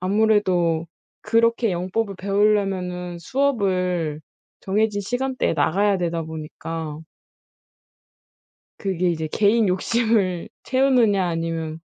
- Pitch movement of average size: Yes, average, 4.3 semitones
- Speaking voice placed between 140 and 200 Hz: Yes, high, 190 Hz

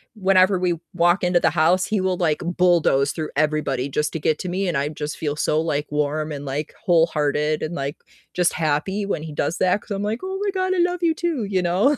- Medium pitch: Yes, medium, 170 Hz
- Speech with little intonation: No, average, 4.2 semitones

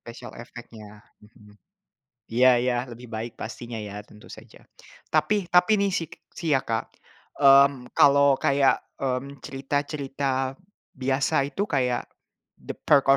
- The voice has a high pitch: No, low, 135 Hz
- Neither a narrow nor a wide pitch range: Yes, average, 3.2 semitones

